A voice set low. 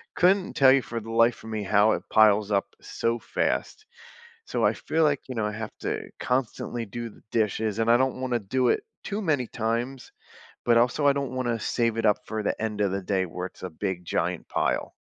Yes: low, 115 Hz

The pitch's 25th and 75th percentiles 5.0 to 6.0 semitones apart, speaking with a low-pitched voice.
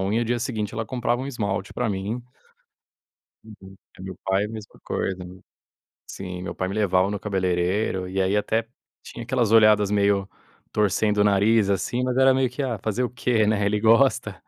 No: average, 3.1 semitones; low, 105 Hz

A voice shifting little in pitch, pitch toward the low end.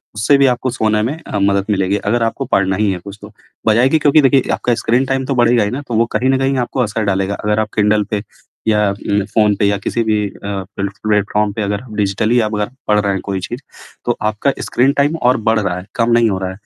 No: average, 3.1 semitones; low, 105 Hz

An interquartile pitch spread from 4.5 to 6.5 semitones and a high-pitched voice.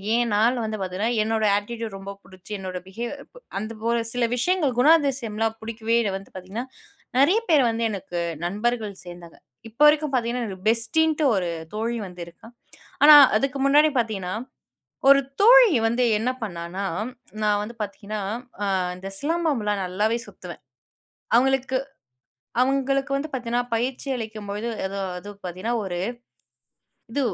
Yes: average, 5.0 semitones; high, 225 Hz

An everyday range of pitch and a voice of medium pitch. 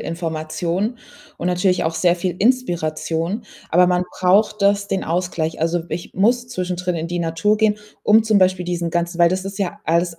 Yes: average, 3.0 semitones; medium, 180 Hz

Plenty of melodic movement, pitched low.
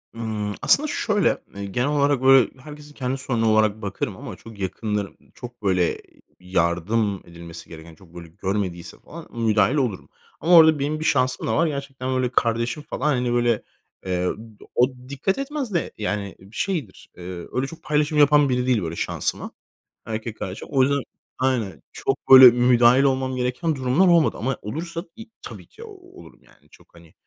Yes: wide, 6.0 semitones; low, 125 Hz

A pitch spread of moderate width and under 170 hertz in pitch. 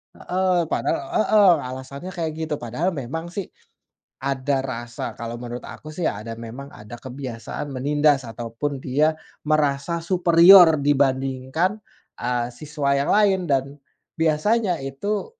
Yes: average, 4.6 semitones; medium, 140 Hz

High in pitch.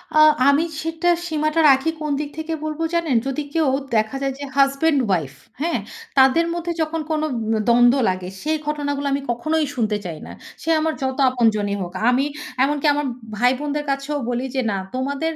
Yes: very high, 280 Hz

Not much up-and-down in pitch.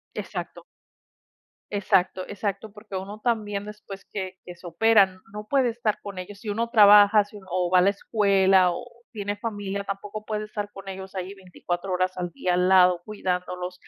Yes: narrow, 2.2 semitones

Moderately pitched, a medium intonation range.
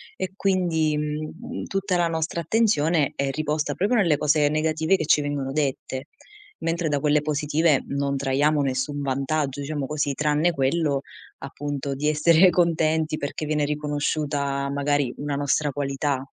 No: medium, 150 Hz; narrow, 2.1 semitones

